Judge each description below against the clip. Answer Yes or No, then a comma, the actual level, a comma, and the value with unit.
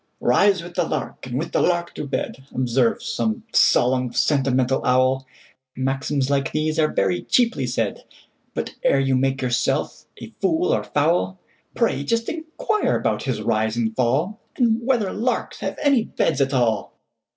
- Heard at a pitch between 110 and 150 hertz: Yes, low, 135 Hz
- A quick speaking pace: No, average, 145 wpm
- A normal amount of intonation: No, wide, 7.5 semitones